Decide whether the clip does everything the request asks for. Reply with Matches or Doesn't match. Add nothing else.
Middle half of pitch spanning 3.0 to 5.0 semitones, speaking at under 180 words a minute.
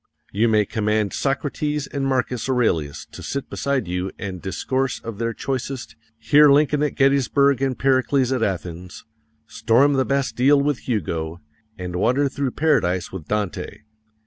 Doesn't match